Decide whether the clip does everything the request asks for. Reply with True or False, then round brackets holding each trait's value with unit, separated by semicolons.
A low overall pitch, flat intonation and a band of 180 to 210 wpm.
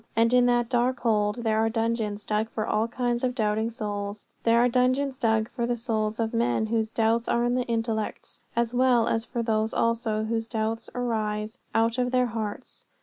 False (230 Hz; 1.7 semitones; 200 wpm)